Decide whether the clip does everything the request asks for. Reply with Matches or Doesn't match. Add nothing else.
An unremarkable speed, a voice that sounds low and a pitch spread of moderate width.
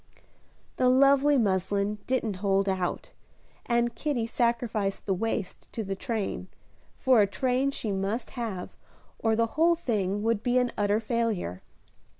Doesn't match